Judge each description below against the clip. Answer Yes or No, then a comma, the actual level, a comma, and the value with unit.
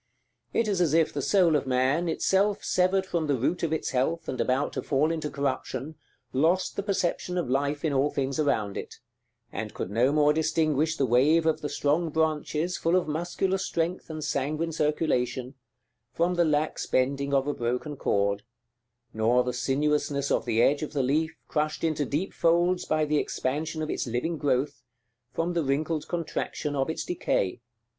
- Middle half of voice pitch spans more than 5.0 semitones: No, average, 3.4 semitones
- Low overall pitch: No, medium, 150 Hz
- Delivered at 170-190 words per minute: Yes, average, 180 wpm